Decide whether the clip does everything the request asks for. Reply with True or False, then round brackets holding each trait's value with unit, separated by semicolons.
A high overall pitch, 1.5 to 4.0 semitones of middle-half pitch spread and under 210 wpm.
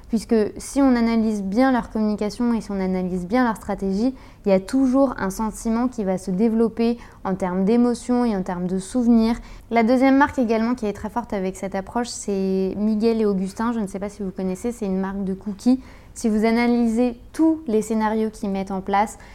False (220 Hz; 3.4 semitones; 215 wpm)